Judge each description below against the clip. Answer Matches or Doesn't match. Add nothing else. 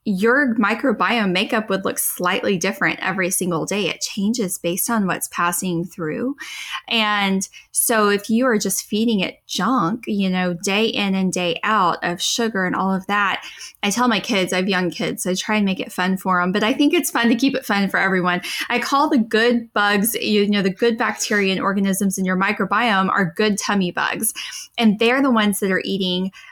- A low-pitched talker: Doesn't match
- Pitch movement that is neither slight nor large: Matches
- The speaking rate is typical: Doesn't match